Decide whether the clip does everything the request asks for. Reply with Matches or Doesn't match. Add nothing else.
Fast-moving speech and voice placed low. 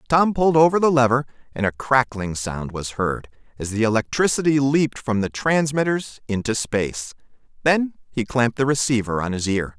Doesn't match